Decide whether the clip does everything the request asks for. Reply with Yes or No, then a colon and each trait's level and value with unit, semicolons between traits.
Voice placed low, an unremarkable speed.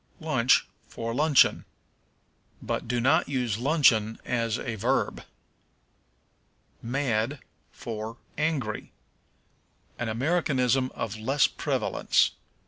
No: low, 125 Hz; slow, 90 wpm